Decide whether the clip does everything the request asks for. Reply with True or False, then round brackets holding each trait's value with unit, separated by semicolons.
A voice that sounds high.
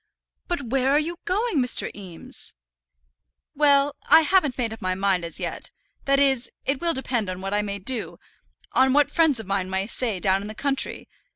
True (255 Hz)